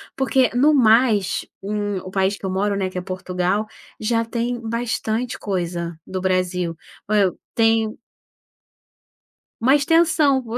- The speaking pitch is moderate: No, high, 210 Hz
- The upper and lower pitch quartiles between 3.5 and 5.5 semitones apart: Yes, average, 4.2 semitones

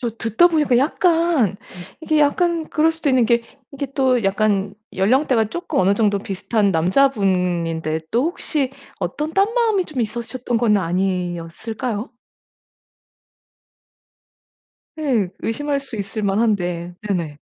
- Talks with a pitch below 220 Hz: No, high, 230 Hz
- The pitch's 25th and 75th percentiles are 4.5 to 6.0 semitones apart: No, wide, 6.8 semitones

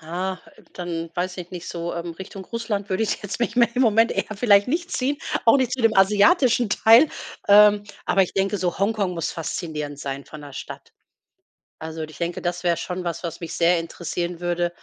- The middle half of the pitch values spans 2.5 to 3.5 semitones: No, average, 4.0 semitones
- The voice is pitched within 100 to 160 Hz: No, medium, 185 Hz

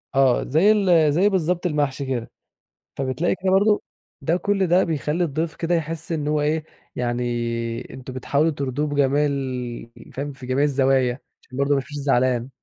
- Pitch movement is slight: No, average, 4.1 semitones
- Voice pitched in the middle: Yes, medium, 145 Hz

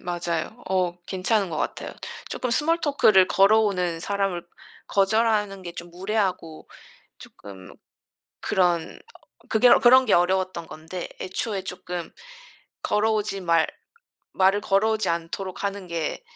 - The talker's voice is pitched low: No, high, 190 Hz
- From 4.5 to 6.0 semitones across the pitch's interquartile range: No, average, 3.3 semitones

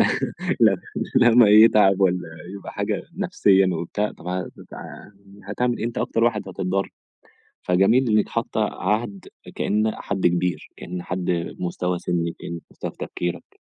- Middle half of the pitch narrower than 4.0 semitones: Yes, average, 3.1 semitones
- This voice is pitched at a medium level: No, very low, 95 Hz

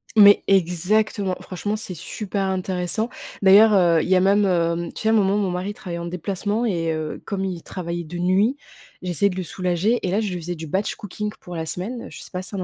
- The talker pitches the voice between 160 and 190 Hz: Yes, medium, 185 Hz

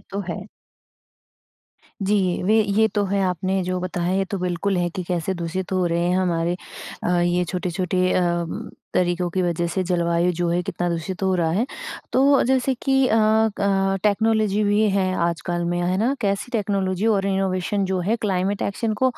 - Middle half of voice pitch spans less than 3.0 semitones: Yes, narrow, 2.6 semitones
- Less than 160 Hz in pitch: No, medium, 185 Hz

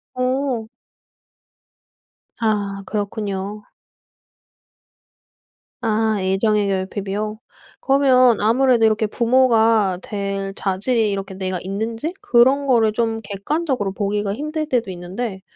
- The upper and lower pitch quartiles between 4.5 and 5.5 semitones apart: No, average, 3.6 semitones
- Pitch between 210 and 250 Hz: Yes, high, 215 Hz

